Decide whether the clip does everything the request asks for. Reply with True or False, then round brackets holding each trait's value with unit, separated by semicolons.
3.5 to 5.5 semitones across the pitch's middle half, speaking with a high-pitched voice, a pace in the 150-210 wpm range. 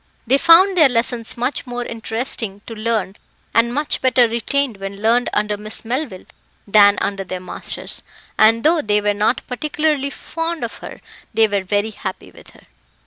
True (4.4 semitones; 230 Hz; 170 wpm)